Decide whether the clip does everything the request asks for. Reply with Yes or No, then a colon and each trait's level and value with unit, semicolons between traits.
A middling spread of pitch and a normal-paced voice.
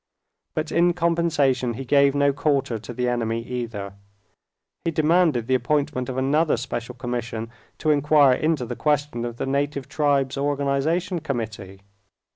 Yes: average, 3.8 semitones; average, 145 wpm